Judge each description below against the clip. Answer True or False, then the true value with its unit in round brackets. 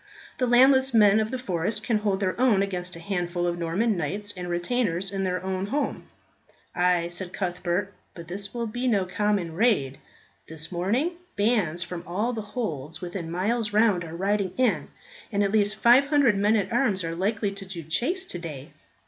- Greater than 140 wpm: True (180 wpm)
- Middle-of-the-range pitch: False (195 Hz)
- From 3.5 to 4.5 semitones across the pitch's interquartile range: True (4.2 semitones)